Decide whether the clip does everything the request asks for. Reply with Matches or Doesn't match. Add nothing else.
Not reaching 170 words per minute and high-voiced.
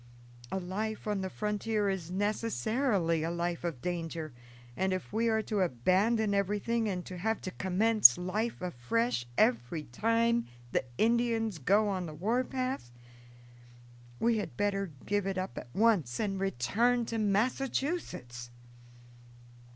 Matches